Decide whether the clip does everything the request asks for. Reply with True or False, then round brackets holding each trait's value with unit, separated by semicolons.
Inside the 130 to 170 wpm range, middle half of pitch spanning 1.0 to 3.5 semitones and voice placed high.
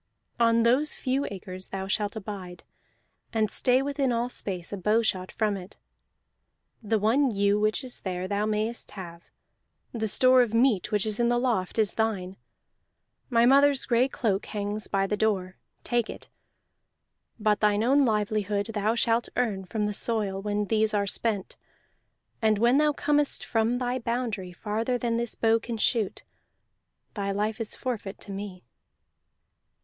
True (160 wpm; 2.8 semitones; 215 Hz)